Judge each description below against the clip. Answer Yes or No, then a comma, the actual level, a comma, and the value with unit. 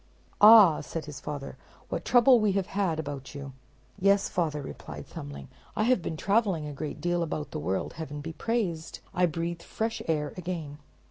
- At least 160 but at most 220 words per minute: Yes, average, 180 wpm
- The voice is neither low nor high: Yes, medium, 165 Hz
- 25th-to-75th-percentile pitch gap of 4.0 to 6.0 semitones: Yes, average, 4.9 semitones